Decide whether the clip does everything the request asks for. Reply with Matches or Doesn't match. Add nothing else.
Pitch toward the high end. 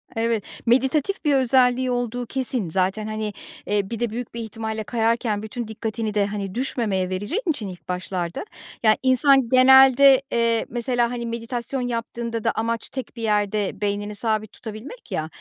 Matches